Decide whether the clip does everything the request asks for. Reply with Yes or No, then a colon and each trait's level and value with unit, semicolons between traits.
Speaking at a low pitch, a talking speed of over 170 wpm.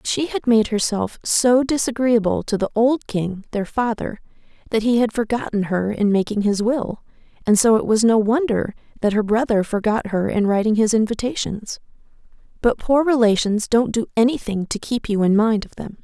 No: high, 220 Hz; average, 185 wpm